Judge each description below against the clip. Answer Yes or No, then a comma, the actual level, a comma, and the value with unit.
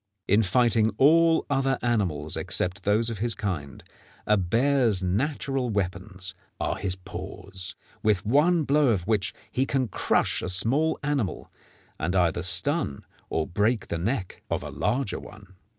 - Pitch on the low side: Yes, low, 105 Hz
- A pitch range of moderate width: No, wide, 6.3 semitones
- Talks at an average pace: Yes, average, 150 wpm